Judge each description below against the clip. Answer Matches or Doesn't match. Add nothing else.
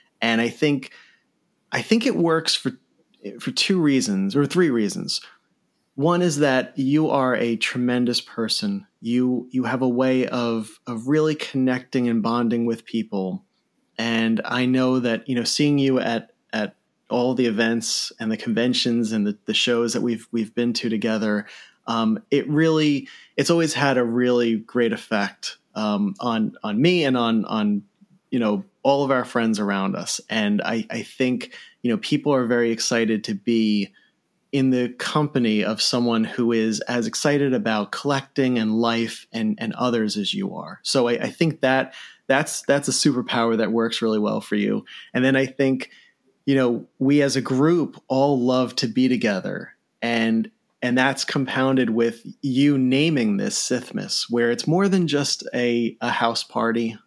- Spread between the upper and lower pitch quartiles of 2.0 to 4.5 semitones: Matches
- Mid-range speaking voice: Doesn't match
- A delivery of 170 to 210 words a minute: Matches